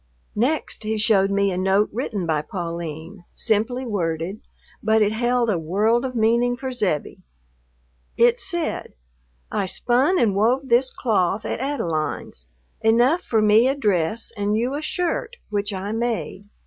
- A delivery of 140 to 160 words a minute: Yes, average, 150 wpm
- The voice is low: No, high, 220 Hz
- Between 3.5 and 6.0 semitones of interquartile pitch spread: Yes, average, 4.3 semitones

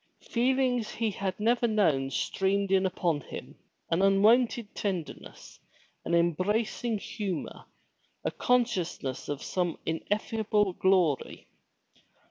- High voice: Yes, high, 195 Hz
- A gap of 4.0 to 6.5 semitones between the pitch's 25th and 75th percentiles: Yes, average, 4.4 semitones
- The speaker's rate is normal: No, slow, 105 wpm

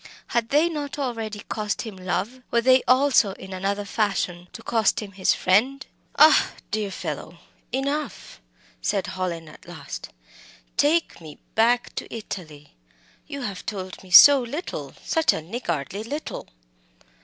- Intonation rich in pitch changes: Yes, wide, 5.9 semitones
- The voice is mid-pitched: No, high, 220 Hz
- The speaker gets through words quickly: No, average, 145 wpm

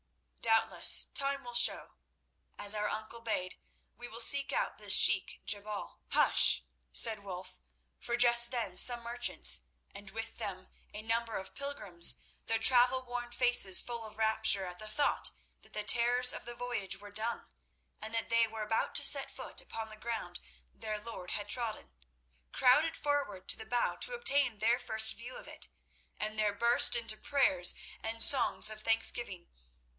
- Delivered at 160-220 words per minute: Yes, average, 170 wpm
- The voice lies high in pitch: Yes, high, 225 Hz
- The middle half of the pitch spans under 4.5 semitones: Yes, narrow, 2.6 semitones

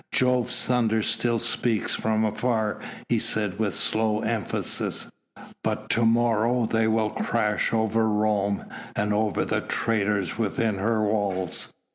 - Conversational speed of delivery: No, slow, 130 wpm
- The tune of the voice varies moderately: No, narrow, 1.5 semitones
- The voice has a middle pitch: No, low, 110 Hz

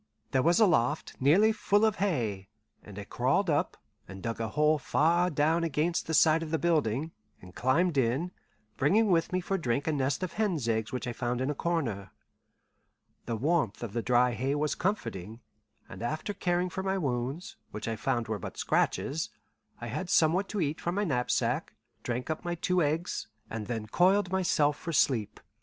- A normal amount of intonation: No, wide, 6.5 semitones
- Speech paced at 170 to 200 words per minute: Yes, average, 190 wpm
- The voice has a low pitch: No, medium, 150 Hz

